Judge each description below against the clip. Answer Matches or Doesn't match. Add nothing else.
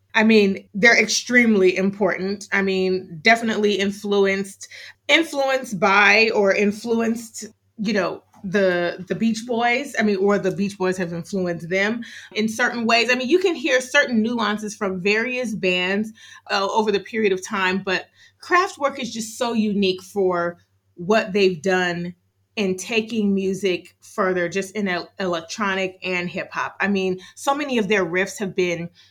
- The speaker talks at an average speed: Matches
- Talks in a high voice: Matches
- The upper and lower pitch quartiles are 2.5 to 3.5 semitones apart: Matches